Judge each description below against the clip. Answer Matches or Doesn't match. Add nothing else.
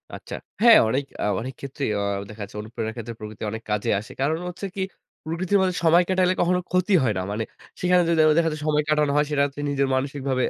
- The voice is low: Doesn't match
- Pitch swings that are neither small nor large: Doesn't match